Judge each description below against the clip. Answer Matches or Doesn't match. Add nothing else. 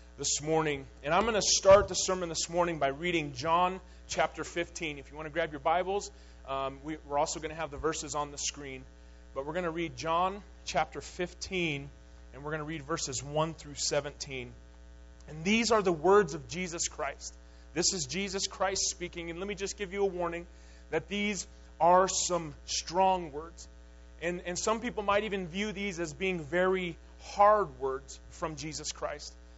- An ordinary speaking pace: Matches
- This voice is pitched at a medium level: Matches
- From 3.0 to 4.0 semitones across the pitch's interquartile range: Doesn't match